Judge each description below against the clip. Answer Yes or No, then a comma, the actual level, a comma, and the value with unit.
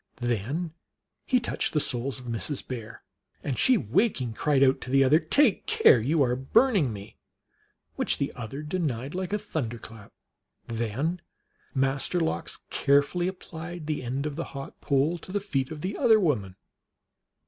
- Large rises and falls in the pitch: Yes, wide, 5.9 semitones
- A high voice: No, medium, 140 Hz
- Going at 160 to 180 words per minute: Yes, average, 170 wpm